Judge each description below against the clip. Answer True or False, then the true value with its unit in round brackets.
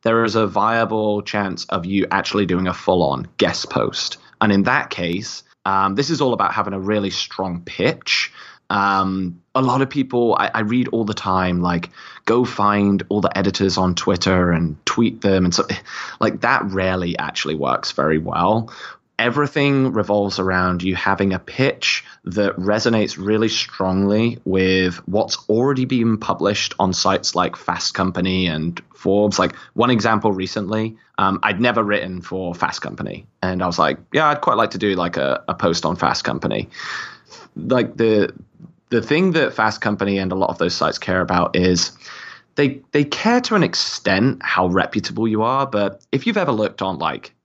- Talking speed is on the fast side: False (180 wpm)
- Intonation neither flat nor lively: True (3.6 semitones)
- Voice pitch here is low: True (100 Hz)